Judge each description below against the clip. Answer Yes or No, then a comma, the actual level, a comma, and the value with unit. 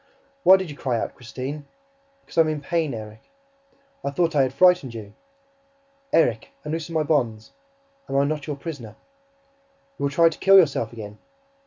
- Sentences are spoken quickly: No, average, 175 wpm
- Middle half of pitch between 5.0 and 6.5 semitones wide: Yes, wide, 5.4 semitones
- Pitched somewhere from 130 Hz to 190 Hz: Yes, medium, 140 Hz